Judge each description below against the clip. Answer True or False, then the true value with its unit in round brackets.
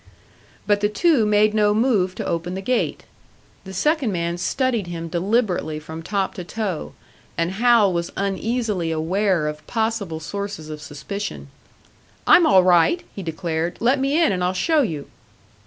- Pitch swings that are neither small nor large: True (4.7 semitones)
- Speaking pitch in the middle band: False (195 Hz)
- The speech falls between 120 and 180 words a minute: True (160 wpm)